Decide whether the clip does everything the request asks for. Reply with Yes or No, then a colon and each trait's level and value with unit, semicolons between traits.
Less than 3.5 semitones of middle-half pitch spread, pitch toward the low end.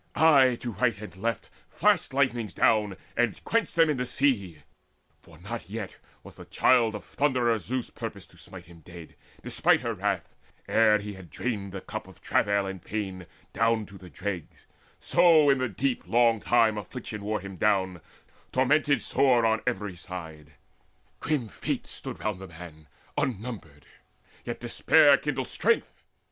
No: average, 4.9 semitones; low, 105 Hz